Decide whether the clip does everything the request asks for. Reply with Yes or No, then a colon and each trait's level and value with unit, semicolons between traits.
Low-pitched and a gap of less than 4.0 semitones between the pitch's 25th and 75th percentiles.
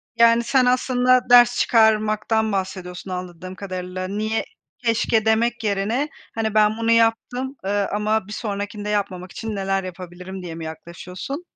No: high, 215 Hz; average, 3.5 semitones